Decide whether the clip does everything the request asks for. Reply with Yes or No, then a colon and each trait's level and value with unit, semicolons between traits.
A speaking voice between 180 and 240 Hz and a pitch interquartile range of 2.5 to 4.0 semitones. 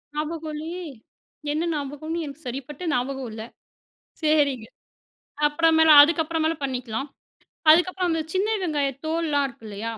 No: very high, 300 Hz; average, 3.3 semitones